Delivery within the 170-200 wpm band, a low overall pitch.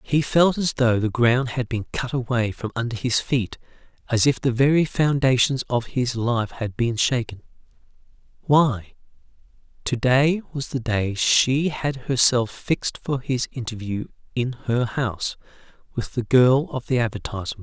No: average, 160 wpm; low, 125 Hz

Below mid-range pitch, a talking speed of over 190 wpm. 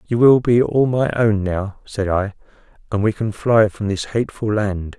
Yes: low, 105 Hz; fast, 205 wpm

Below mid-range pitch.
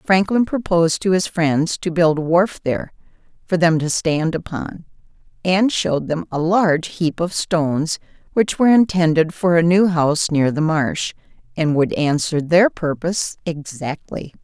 No: medium, 165 Hz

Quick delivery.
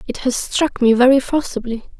No: average, 180 wpm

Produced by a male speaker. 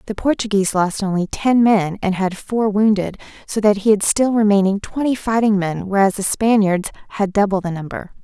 No: female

